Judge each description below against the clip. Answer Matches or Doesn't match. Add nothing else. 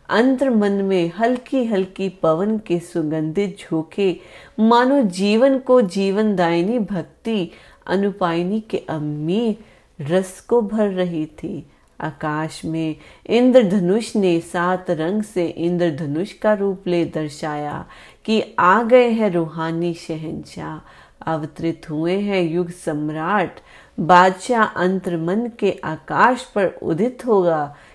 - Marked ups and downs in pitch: Doesn't match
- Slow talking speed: Matches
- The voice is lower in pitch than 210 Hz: Matches